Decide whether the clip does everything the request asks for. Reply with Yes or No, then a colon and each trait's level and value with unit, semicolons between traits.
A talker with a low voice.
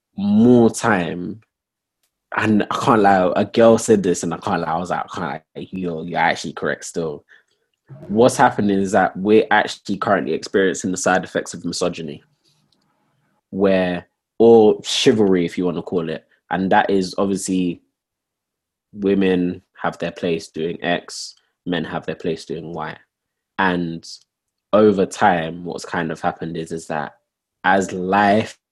Yes: very low, 95 Hz